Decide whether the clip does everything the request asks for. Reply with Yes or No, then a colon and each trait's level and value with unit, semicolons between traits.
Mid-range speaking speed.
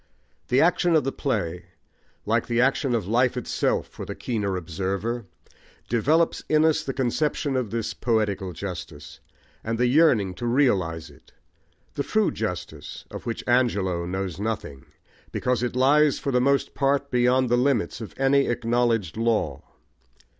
Yes: average, 155 wpm